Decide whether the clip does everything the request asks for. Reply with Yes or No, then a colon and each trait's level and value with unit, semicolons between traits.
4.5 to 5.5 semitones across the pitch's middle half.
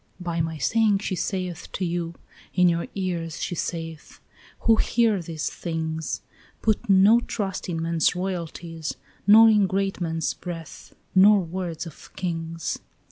No: average, 2.9 semitones